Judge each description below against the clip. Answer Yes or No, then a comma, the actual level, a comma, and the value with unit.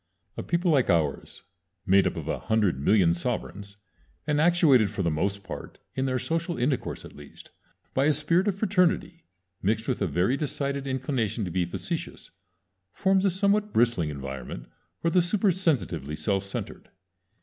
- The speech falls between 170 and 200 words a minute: No, average, 160 wpm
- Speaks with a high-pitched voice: No, low, 130 Hz